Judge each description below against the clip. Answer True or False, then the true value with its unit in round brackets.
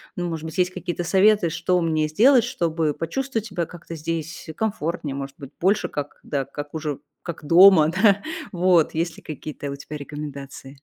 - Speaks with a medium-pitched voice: True (165 Hz)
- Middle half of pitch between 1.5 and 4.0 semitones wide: True (3.5 semitones)